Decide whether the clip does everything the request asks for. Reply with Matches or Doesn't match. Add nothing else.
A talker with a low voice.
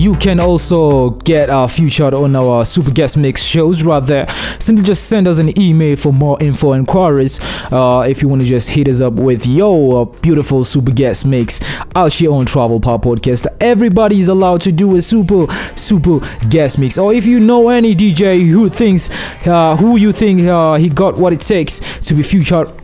Doesn't match